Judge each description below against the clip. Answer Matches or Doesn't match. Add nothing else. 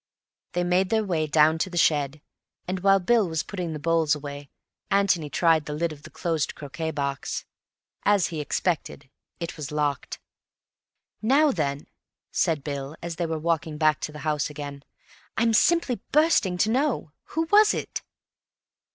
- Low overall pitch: Doesn't match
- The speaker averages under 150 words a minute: Doesn't match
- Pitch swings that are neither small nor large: Matches